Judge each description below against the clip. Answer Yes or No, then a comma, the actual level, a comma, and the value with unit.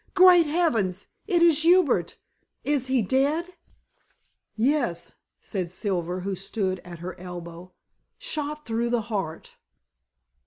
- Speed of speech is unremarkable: No, slow, 115 wpm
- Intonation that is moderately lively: No, wide, 8.7 semitones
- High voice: Yes, high, 225 Hz